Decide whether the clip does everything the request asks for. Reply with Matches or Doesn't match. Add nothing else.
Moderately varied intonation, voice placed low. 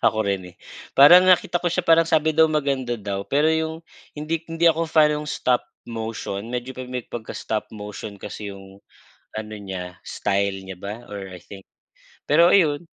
Doesn't match